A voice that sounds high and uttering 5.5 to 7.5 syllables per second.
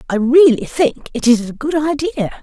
No: very high, 275 Hz; 5.2 syllables/s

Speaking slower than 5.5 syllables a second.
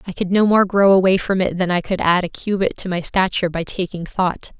No: 5.7 syllables/s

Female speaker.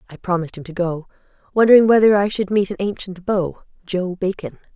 Yes: female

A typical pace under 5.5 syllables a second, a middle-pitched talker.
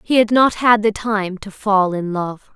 No: 4.1 syllables/s; high, 210 Hz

